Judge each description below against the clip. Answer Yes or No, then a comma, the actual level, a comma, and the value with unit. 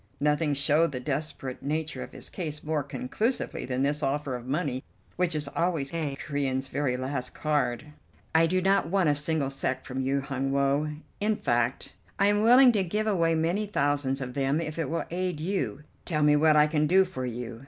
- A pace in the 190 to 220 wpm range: Yes, average, 200 wpm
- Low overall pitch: No, medium, 150 Hz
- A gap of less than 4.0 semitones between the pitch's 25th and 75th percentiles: Yes, average, 3.6 semitones